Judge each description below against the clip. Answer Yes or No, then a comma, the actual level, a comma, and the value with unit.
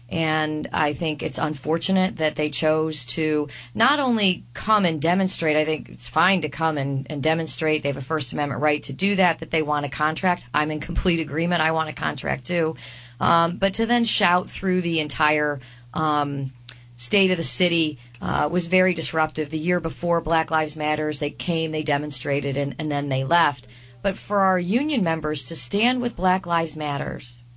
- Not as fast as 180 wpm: No, average, 195 wpm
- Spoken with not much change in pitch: No, average, 3.0 semitones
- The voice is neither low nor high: Yes, medium, 155 Hz